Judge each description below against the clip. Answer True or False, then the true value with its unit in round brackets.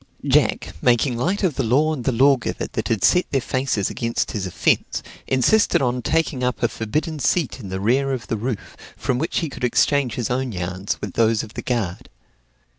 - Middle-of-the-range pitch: False (125 Hz)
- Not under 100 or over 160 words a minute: False (200 wpm)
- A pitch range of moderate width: True (3.6 semitones)